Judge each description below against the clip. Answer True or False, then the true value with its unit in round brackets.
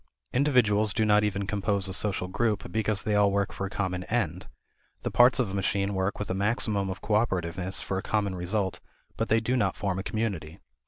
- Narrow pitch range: True (2.2 semitones)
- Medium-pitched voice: False (100 Hz)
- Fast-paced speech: True (210 wpm)